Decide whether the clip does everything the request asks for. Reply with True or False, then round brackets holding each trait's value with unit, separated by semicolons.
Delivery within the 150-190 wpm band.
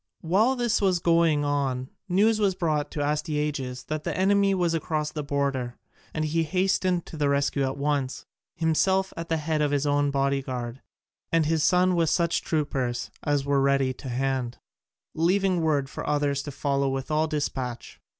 True (180 wpm)